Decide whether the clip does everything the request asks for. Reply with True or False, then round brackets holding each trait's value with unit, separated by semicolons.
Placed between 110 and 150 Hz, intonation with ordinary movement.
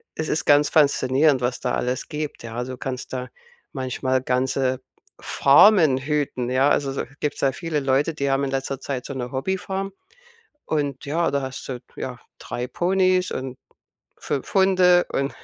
True (135 Hz; 3.1 semitones)